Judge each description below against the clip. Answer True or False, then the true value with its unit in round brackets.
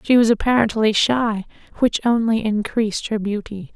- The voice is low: False (220 Hz)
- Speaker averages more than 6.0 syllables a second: False (4.9 syllables/s)